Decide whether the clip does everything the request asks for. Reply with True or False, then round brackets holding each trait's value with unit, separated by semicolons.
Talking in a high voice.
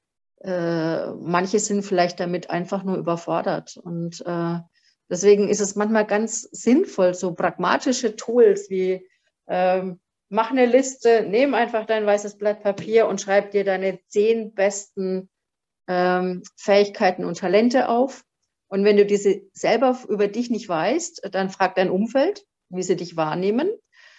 True (200 Hz)